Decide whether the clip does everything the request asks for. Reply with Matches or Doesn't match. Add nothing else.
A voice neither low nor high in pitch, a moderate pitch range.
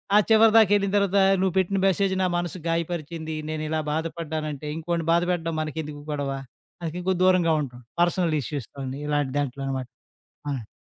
Matches